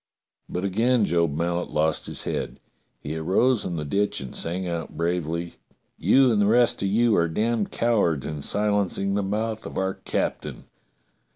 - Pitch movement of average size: Yes, average, 4.5 semitones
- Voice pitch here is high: No, very low, 95 Hz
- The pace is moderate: Yes, average, 175 wpm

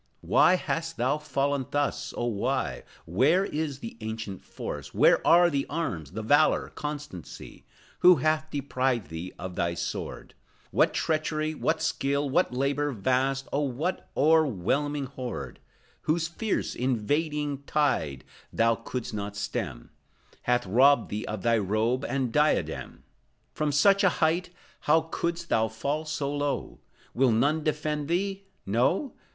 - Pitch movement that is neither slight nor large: Yes, average, 5.0 semitones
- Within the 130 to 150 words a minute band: Yes, average, 140 wpm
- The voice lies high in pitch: No, medium, 140 Hz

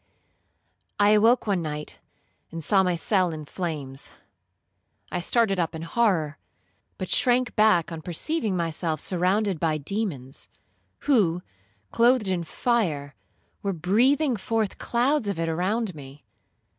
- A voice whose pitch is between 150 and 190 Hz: Yes, medium, 185 Hz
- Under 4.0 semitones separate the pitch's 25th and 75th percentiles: No, wide, 5.4 semitones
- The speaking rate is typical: No, slow, 130 wpm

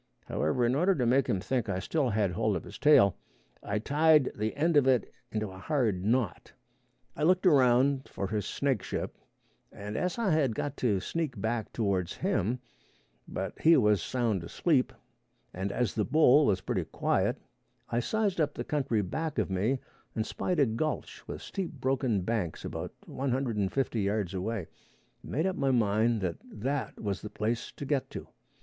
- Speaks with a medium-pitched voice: No, low, 120 Hz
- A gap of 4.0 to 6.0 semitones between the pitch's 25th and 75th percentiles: Yes, wide, 5.5 semitones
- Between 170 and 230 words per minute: Yes, average, 180 wpm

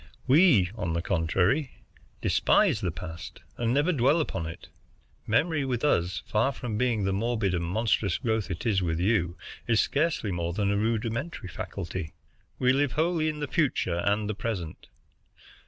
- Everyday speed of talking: Yes, average, 165 wpm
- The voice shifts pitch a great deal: Yes, wide, 6.6 semitones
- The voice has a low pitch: Yes, low, 110 Hz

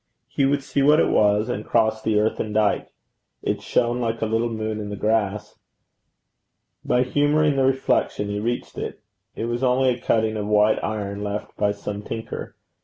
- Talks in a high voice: No, low, 110 Hz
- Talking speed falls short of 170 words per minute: No, average, 180 wpm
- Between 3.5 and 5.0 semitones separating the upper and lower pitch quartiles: No, average, 3.0 semitones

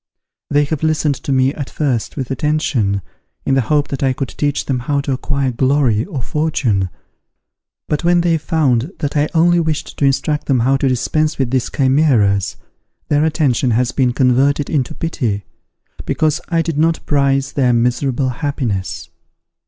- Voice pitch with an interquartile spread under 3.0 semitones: No, average, 3.3 semitones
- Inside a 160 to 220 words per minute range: Yes, average, 170 wpm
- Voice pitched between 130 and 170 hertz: Yes, medium, 140 Hz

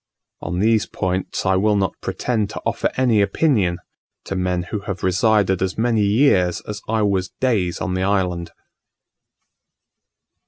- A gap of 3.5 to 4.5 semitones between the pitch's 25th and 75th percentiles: No, average, 2.9 semitones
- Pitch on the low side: Yes, low, 100 Hz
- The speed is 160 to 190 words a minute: No, average, 150 wpm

